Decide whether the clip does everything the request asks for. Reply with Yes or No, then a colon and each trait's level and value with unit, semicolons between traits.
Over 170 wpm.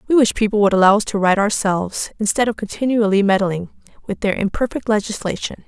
Yes: average, 180 wpm